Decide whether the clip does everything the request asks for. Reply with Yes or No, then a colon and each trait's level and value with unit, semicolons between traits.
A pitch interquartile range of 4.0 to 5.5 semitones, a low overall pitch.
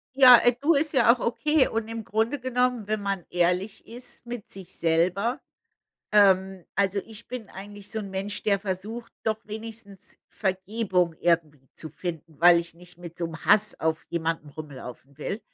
No: average, 4.7 semitones; high, 200 Hz